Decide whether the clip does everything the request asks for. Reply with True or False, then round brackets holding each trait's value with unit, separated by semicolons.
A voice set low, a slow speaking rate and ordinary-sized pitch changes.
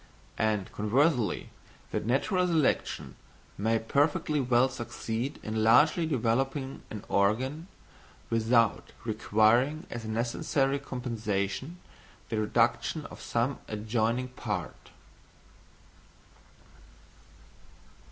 True (120 Hz; 85 wpm; 3.8 semitones)